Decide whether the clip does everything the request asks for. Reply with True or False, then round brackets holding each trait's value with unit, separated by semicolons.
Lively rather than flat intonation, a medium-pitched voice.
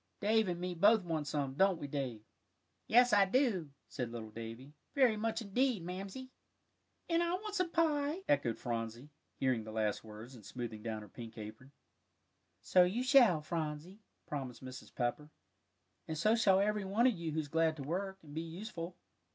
True (9.0 semitones; 165 Hz)